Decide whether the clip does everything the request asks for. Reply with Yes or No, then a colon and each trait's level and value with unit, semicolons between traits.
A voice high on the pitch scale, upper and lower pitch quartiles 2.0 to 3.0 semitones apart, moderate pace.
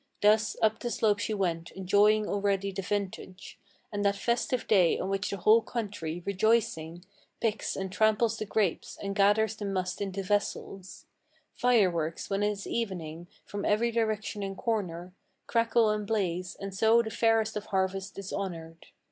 Yes: high, 200 Hz; narrow, 2.5 semitones; average, 165 wpm